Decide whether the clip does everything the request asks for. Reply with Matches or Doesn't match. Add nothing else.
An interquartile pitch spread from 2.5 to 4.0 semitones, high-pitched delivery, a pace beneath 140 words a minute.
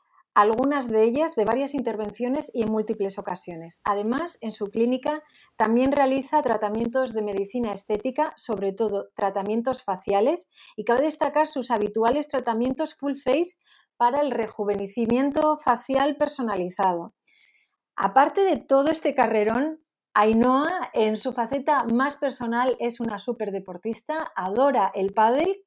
Doesn't match